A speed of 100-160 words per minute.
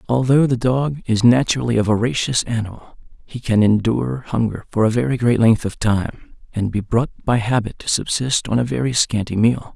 No: average, 190 wpm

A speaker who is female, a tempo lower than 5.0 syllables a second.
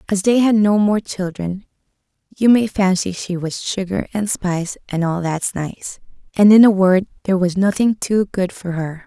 Yes: female; 4.7 syllables/s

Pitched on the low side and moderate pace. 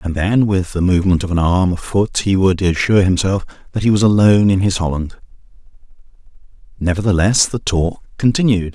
Yes: very low, 95 Hz; average, 170 wpm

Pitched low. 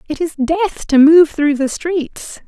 No: very high, 310 Hz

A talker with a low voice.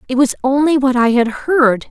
No: very high, 260 Hz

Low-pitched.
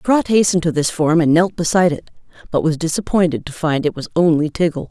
No: medium, 165 Hz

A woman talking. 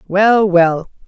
Yes: female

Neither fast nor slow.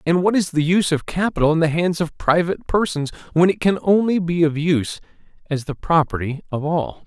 No: fast, 210 wpm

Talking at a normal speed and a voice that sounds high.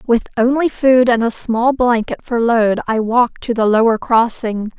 Yes: average, 190 wpm; high, 235 Hz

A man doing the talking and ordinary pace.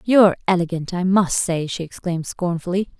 No: female; average, 160 wpm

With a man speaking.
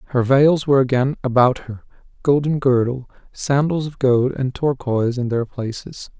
Yes: male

